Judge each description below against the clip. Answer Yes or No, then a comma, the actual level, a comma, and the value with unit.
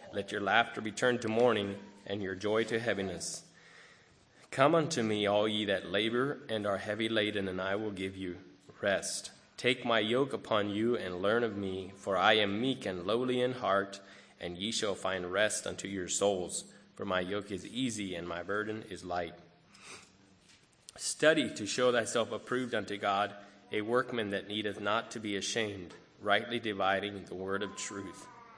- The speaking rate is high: No, average, 180 wpm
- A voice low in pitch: Yes, low, 105 Hz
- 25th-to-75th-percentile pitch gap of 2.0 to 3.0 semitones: Yes, narrow, 2.5 semitones